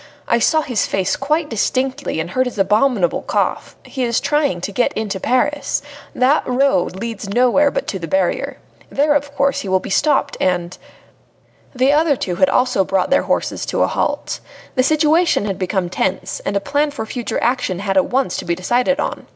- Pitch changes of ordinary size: No, wide, 6.5 semitones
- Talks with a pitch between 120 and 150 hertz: No, high, 245 Hz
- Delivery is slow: No, average, 200 wpm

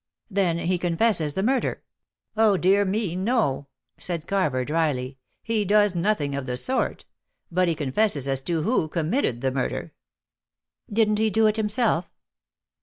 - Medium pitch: Yes, medium, 180 Hz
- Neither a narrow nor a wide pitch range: No, wide, 6.1 semitones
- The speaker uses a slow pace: No, average, 150 wpm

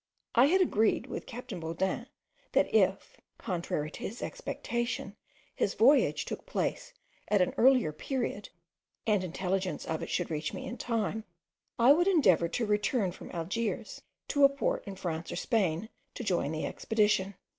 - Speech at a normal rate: Yes, average, 160 wpm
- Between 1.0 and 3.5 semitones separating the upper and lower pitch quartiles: No, wide, 5.5 semitones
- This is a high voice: Yes, high, 210 Hz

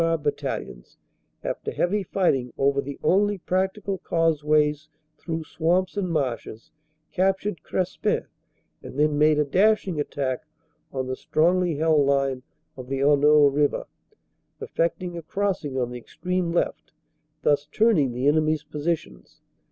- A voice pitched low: No, medium, 155 Hz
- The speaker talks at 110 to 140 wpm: Yes, slow, 135 wpm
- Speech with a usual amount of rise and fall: Yes, average, 4.2 semitones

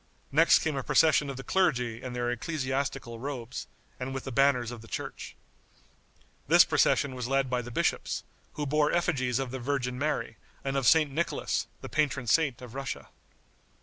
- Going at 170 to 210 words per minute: Yes, average, 180 wpm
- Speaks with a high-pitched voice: No, low, 135 Hz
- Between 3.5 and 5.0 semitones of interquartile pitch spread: No, average, 2.7 semitones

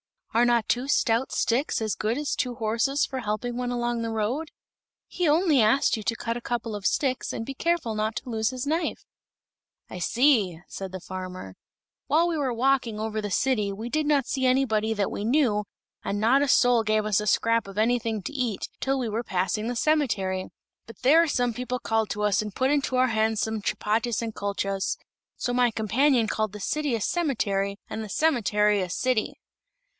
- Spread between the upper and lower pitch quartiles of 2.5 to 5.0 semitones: Yes, average, 3.6 semitones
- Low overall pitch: No, high, 230 Hz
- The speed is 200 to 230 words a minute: Yes, fast, 205 wpm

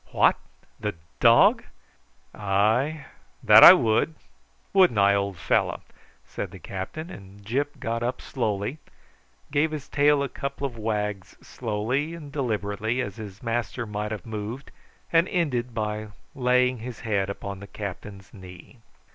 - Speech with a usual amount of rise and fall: Yes, average, 4.9 semitones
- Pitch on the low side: Yes, low, 115 Hz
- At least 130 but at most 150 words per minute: Yes, average, 140 wpm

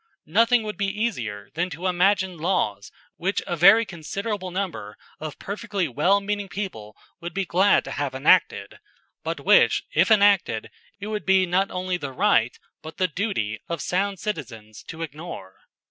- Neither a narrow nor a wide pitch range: Yes, average, 4.8 semitones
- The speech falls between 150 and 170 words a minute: Yes, average, 160 wpm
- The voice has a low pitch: No, medium, 185 Hz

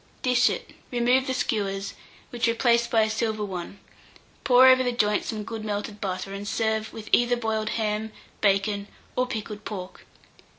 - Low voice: No, high, 220 Hz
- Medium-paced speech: Yes, average, 165 wpm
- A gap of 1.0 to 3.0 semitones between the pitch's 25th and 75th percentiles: Yes, narrow, 2.6 semitones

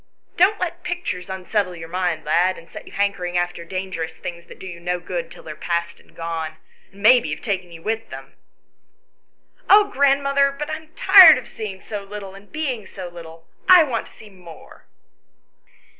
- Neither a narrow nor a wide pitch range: No, wide, 6.9 semitones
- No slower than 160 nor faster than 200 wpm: Yes, average, 190 wpm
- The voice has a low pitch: No, high, 190 Hz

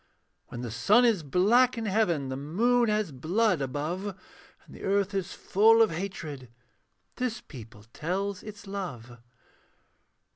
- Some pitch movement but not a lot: No, wide, 6.9 semitones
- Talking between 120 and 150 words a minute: Yes, average, 140 wpm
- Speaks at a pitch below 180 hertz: No, high, 190 Hz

